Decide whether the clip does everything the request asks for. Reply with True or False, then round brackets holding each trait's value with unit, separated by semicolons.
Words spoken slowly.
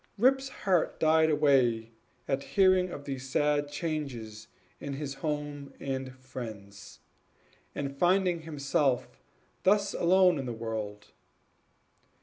True (115 wpm)